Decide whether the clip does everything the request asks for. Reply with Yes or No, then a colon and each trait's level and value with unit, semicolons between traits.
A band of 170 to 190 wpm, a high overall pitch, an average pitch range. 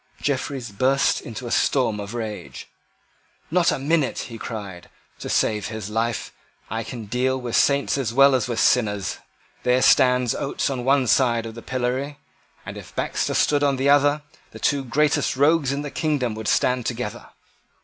No: average, 175 wpm; low, 125 Hz; average, 3.5 semitones